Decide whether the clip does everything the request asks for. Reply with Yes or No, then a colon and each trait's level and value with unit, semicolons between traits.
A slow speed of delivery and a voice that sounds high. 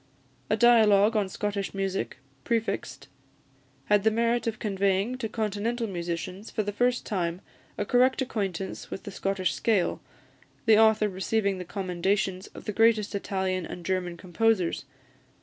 No: average, 145 wpm; high, 205 Hz